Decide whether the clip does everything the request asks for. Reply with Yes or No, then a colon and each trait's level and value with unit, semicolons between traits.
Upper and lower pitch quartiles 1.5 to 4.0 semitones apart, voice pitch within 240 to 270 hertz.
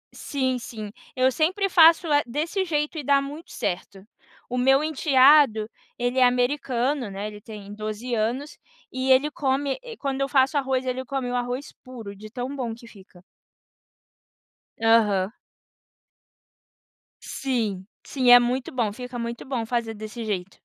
Yes: average, 3.7 semitones; very high, 250 Hz